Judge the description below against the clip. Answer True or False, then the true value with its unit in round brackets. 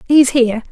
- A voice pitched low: False (255 Hz)